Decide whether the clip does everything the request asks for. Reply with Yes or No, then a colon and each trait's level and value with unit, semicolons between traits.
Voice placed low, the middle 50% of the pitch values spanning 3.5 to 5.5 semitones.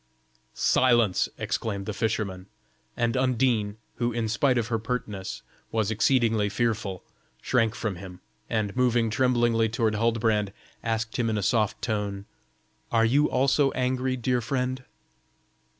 No: low, 115 Hz; average, 2.9 semitones